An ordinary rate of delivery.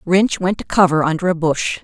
No: fast, 230 wpm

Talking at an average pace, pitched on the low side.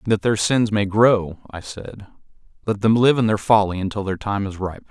No: fast, 230 wpm; low, 105 Hz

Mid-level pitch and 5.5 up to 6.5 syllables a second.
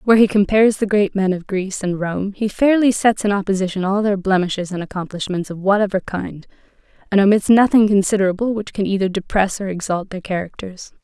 No: high, 195 Hz; 6.0 syllables/s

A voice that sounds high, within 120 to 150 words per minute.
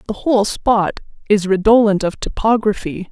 Yes: high, 210 Hz; slow, 135 wpm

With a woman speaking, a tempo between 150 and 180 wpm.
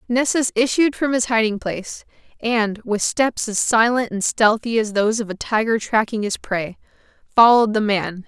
Yes: female; average, 175 wpm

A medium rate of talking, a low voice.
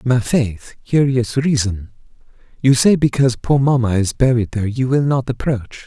Yes: average, 165 wpm; low, 125 Hz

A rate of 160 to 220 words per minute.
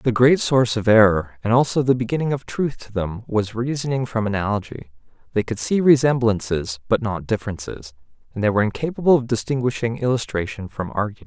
Yes: average, 175 wpm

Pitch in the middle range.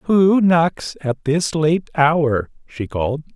Yes: medium, 155 Hz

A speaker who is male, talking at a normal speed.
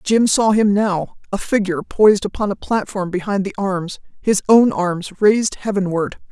No: female; average, 170 wpm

